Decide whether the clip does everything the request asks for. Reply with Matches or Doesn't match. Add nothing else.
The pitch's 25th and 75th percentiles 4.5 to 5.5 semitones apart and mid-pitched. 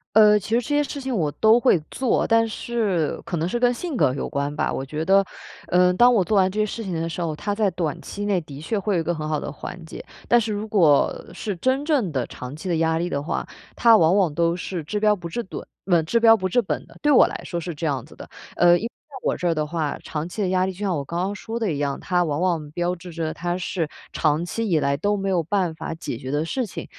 Matches